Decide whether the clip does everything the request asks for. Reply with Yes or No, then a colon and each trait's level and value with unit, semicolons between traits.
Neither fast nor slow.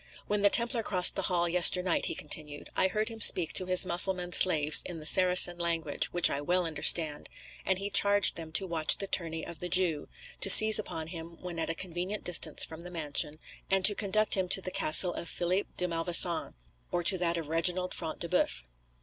No: fast, 210 wpm